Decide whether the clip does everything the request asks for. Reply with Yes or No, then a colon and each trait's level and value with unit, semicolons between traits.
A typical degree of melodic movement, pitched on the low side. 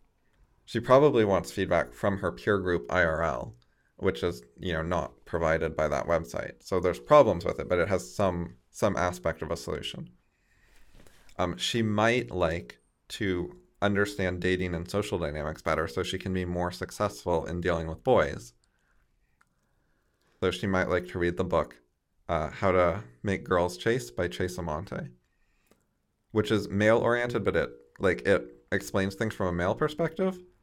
Yes: average, 4.1 semitones; very low, 90 Hz